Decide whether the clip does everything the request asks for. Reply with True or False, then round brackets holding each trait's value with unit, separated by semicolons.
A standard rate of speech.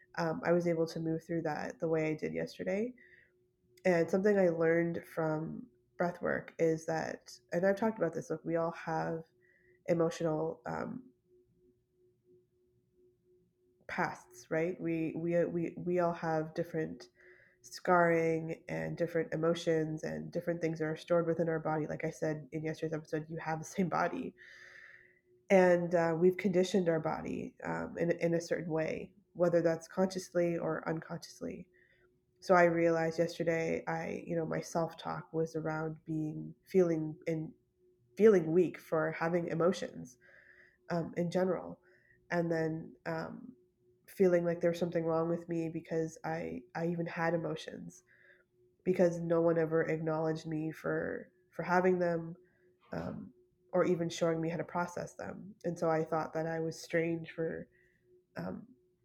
True (155 wpm)